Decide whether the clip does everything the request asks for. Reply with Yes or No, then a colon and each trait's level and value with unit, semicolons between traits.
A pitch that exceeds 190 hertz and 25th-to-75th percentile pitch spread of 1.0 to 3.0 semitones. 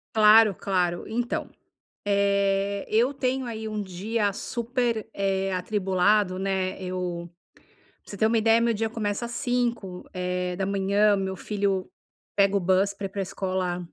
Yes: high, 200 Hz; average, 2.7 semitones